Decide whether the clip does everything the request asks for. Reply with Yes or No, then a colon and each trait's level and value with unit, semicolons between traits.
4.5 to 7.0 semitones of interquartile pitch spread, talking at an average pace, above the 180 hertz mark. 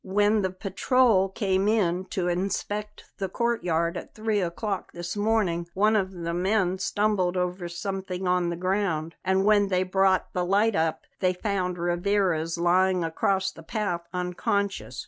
No: narrow, 2.5 semitones; average, 155 wpm; high, 190 Hz